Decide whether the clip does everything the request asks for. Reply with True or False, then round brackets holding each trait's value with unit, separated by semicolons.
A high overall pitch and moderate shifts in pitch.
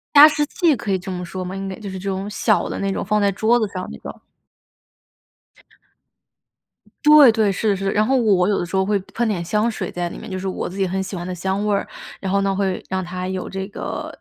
False (195 Hz; 2.1 semitones)